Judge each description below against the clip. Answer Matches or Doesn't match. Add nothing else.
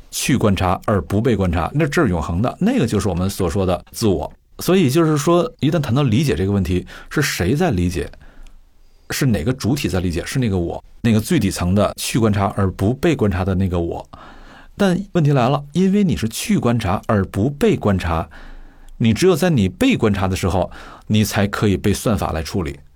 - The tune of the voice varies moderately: Doesn't match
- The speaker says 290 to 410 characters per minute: Matches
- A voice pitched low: Matches